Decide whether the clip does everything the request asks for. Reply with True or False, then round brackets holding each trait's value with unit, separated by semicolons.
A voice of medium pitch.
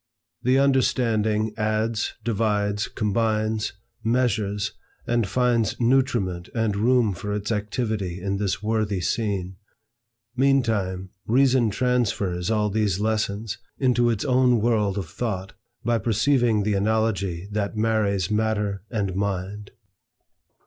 False (110 Hz)